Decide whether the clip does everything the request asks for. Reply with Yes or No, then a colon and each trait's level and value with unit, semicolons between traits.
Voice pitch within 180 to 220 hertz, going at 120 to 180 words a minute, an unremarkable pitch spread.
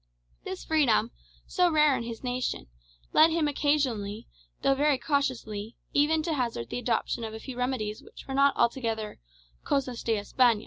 No: very high, 255 Hz; average, 165 wpm; average, 4.3 semitones